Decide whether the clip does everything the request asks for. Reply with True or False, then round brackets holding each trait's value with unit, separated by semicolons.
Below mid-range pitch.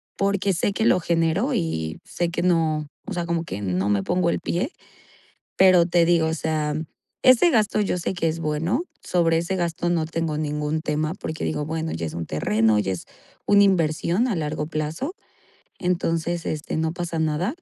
False (165 Hz)